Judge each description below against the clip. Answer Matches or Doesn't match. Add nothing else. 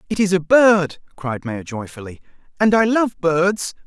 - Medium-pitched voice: Matches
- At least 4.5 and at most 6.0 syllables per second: Doesn't match